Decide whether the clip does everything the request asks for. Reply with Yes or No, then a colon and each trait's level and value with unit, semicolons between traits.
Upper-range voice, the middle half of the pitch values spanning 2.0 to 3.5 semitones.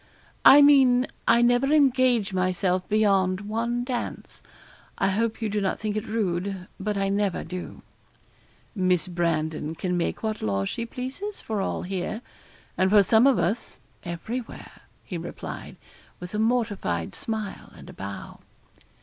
No: high, 205 Hz; average, 4.4 semitones